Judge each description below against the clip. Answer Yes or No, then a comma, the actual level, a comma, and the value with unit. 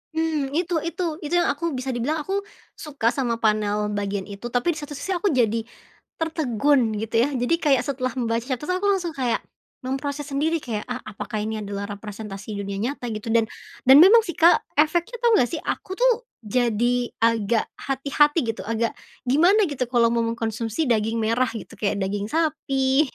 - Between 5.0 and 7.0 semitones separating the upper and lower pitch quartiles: Yes, wide, 5.6 semitones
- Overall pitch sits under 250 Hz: No, very high, 255 Hz